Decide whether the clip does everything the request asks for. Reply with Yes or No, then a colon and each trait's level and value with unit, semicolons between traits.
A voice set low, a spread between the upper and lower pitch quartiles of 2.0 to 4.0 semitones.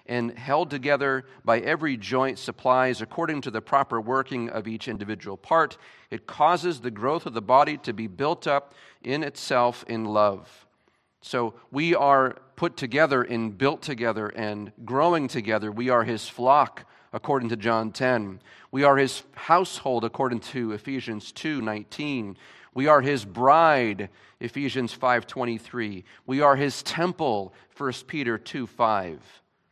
Yes: low, 125 Hz; average, 3.6 semitones